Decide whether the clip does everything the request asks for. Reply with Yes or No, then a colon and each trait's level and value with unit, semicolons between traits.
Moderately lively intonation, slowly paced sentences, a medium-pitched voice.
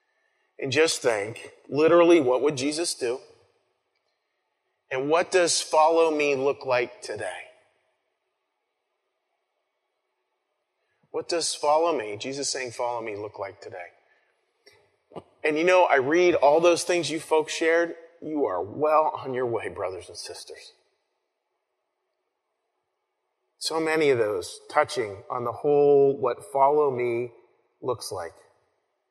Yes: average, 3.8 semitones; slow, 125 wpm; medium, 155 Hz